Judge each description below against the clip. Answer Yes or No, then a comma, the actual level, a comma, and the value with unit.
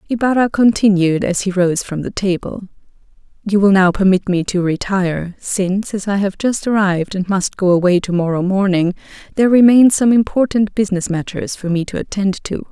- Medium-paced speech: Yes, average, 180 wpm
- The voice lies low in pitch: No, high, 195 Hz